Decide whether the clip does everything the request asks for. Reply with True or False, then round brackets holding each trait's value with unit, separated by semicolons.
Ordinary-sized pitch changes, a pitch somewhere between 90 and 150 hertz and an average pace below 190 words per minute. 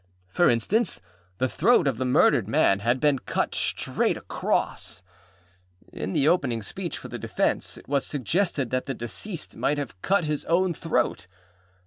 False (6.1 semitones; 140 Hz; 160 wpm)